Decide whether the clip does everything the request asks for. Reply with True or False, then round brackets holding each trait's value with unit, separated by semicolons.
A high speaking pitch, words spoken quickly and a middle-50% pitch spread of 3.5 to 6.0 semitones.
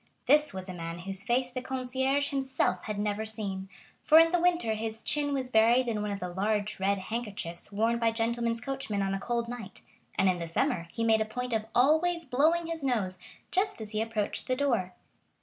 True (230 Hz; 210 wpm; 4.6 semitones)